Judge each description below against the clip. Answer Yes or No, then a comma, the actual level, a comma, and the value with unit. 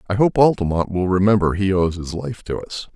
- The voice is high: No, low, 100 Hz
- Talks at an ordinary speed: No, fast, 225 wpm